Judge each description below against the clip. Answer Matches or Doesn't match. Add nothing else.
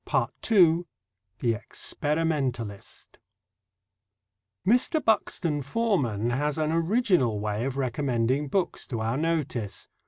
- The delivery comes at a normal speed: Doesn't match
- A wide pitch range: Matches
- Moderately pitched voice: Matches